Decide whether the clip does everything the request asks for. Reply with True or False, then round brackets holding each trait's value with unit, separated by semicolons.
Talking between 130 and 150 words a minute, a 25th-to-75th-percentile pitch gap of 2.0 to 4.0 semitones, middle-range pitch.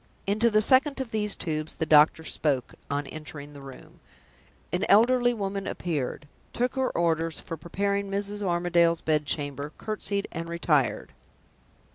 False (145 wpm; 5.2 semitones; 170 Hz)